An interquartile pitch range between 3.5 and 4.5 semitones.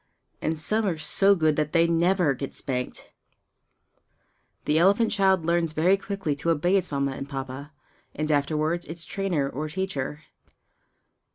Yes: average, 4.2 semitones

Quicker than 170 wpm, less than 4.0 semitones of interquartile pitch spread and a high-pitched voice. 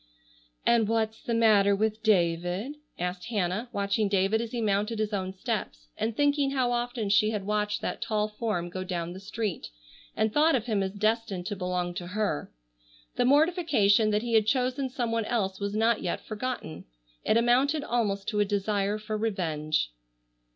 Yes: average, 180 wpm; average, 3.0 semitones; high, 215 Hz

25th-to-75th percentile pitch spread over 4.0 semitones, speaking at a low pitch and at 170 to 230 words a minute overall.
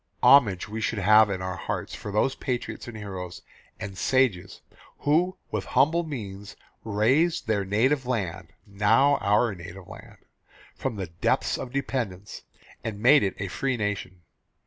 No: average, 5.1 semitones; low, 105 Hz; average, 150 wpm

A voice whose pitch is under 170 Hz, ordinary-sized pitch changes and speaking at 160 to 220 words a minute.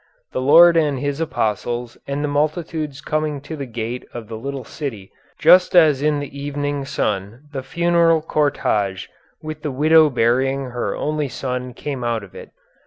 Yes: medium, 140 Hz; average, 3.7 semitones; average, 170 wpm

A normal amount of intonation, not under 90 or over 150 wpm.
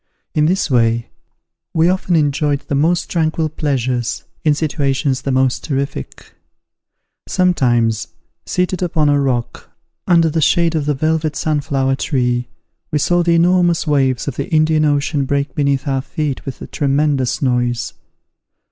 Yes: average, 3.4 semitones; average, 145 wpm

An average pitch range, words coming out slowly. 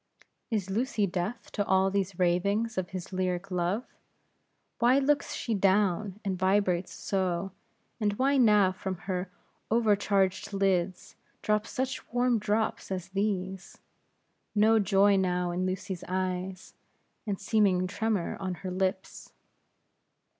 No: narrow, 2.3 semitones; slow, 130 wpm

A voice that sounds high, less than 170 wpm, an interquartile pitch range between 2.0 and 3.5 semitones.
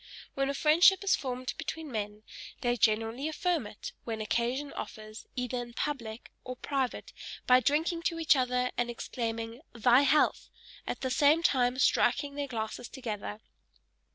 No: very high, 250 Hz; average, 155 wpm; average, 3.9 semitones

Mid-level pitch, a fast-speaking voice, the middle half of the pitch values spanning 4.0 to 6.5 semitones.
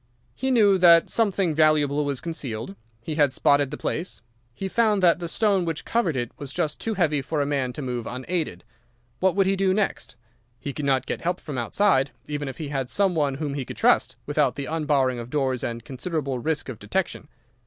Yes: medium, 150 Hz; fast, 210 wpm; average, 5.0 semitones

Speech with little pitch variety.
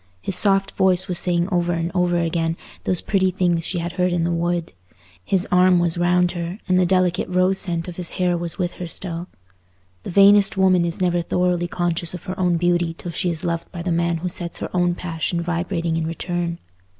Yes: narrow, 1.2 semitones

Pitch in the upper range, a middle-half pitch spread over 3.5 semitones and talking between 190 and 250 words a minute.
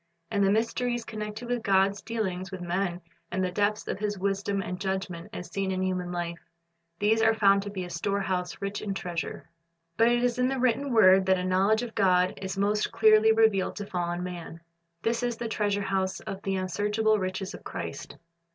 No: high, 195 Hz; average, 2.8 semitones; average, 200 wpm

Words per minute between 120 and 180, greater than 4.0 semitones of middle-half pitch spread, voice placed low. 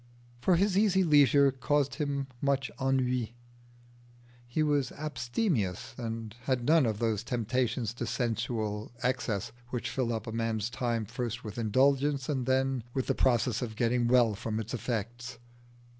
No: average, 150 wpm; average, 3.1 semitones; low, 125 Hz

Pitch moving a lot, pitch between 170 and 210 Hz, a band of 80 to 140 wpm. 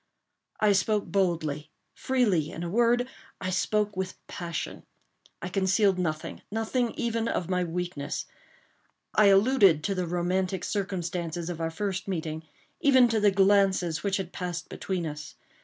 No: average, 3.1 semitones; medium, 185 Hz; slow, 135 wpm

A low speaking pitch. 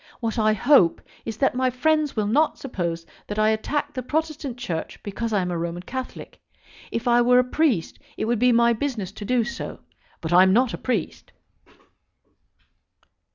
No: high, 235 Hz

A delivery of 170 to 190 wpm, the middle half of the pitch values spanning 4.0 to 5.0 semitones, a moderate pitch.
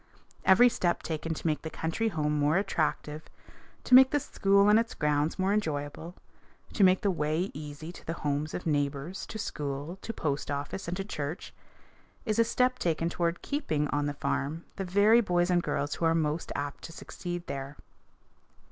Yes: average, 185 wpm; average, 4.6 semitones; medium, 165 Hz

